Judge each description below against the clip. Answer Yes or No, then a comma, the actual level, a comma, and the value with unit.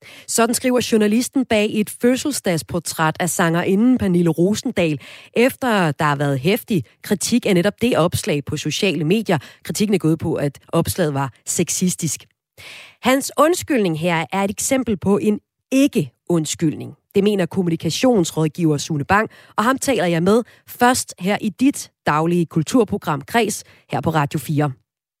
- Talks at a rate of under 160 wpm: Yes, slow, 145 wpm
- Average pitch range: No, wide, 5.7 semitones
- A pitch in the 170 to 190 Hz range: Yes, medium, 185 Hz